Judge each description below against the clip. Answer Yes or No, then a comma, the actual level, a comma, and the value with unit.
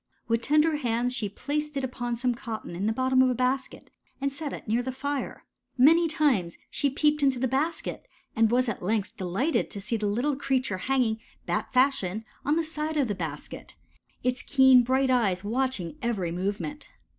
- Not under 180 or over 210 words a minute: Yes, average, 190 wpm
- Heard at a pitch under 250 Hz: No, very high, 255 Hz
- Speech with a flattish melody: No, average, 4.0 semitones